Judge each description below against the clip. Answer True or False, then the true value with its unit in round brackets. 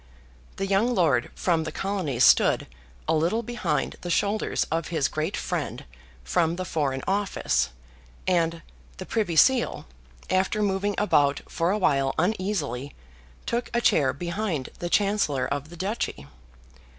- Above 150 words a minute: False (140 wpm)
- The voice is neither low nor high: True (175 Hz)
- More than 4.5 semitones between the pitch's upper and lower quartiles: True (5.4 semitones)